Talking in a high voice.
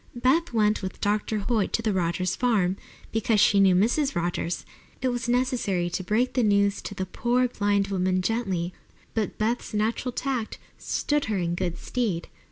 Yes: high, 210 Hz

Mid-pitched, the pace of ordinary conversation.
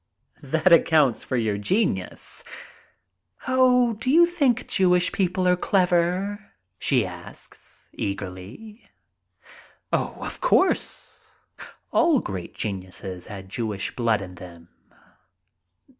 No: medium, 160 Hz; slow, 100 wpm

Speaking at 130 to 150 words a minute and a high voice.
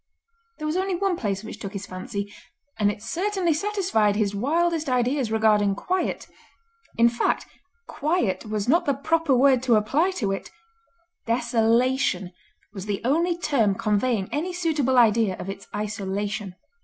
Yes: average, 145 wpm; high, 240 Hz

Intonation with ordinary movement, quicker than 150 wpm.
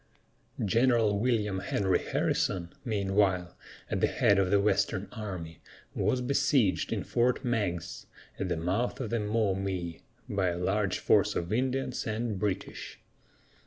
No: average, 3.9 semitones; slow, 135 wpm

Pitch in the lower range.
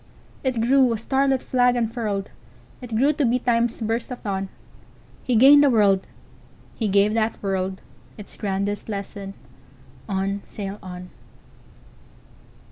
No: high, 220 Hz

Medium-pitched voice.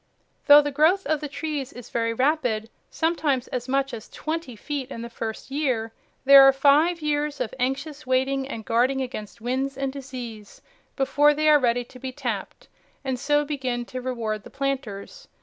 No: very high, 270 Hz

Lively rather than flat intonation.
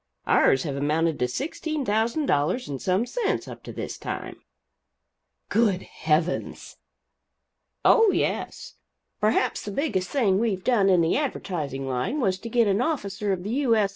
Yes: wide, 6.6 semitones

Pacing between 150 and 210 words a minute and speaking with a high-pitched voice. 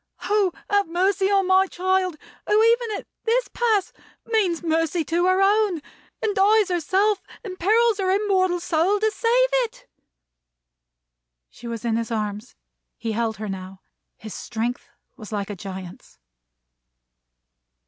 No: average, 140 wpm; very high, 370 Hz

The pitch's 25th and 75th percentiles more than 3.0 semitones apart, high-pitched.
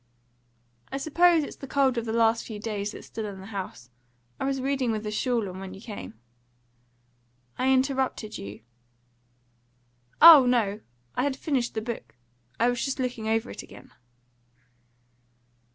Yes: average, 4.0 semitones; high, 235 Hz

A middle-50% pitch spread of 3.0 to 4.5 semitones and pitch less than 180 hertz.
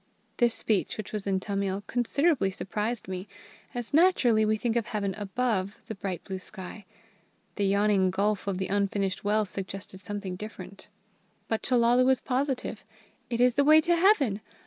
No: average, 3.8 semitones; high, 210 Hz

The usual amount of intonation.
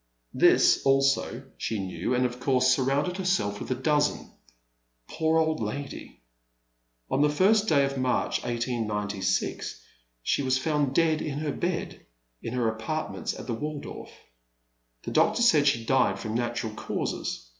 Yes: average, 4.6 semitones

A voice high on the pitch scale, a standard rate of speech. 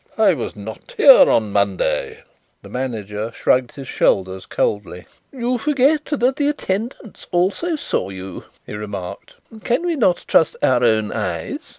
No: low, 130 Hz; average, 145 wpm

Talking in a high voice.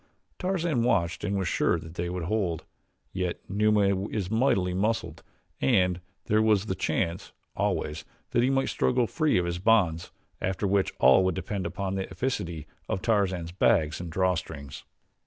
No: very low, 95 Hz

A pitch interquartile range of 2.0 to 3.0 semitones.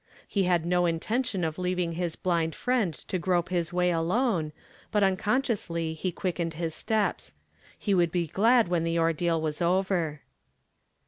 Yes: narrow, 2.5 semitones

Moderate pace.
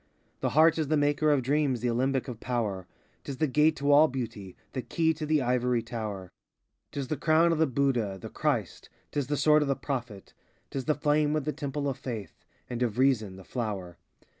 No: fast, 225 wpm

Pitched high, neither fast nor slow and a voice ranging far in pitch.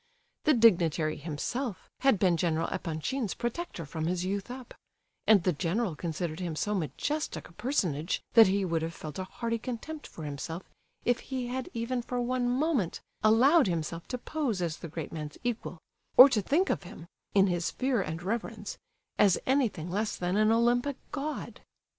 Yes: high, 205 Hz; average, 170 wpm; wide, 6.7 semitones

